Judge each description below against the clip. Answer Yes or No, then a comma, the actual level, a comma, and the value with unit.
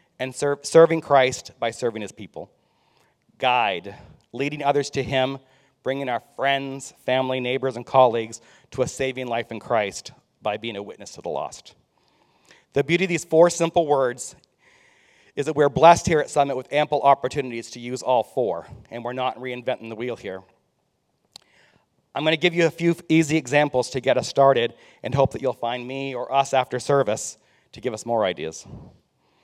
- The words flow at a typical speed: Yes, average, 180 wpm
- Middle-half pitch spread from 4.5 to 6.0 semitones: No, average, 3.2 semitones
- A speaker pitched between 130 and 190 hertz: Yes, low, 135 Hz